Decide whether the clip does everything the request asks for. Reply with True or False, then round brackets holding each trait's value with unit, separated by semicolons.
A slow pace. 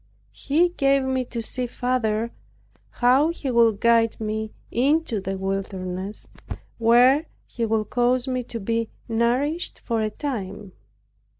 True (130 wpm)